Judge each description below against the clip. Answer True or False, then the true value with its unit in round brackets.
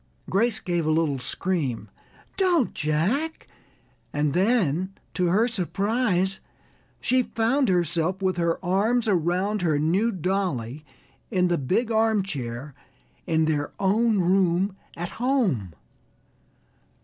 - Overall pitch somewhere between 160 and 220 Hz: True (185 Hz)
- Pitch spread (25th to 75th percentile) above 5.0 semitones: True (5.4 semitones)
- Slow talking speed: True (115 wpm)